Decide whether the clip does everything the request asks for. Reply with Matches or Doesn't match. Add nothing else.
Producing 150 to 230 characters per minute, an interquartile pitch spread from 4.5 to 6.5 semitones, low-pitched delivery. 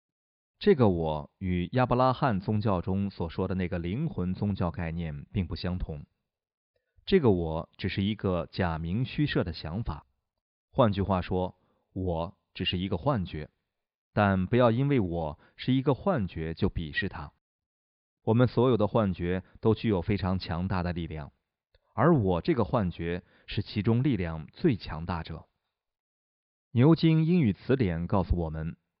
Matches